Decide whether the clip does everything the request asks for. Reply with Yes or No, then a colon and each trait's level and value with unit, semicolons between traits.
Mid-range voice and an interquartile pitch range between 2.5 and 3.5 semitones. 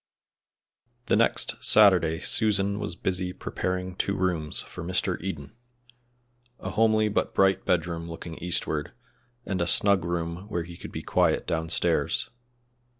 No: very low, 90 Hz; average, 3.0 semitones